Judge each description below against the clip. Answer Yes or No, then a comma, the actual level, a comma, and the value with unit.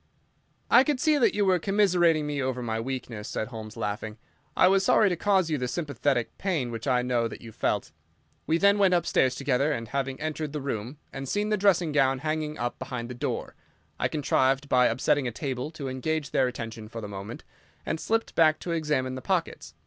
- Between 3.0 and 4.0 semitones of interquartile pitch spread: No, average, 5.0 semitones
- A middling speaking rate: No, fast, 210 wpm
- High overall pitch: No, medium, 140 Hz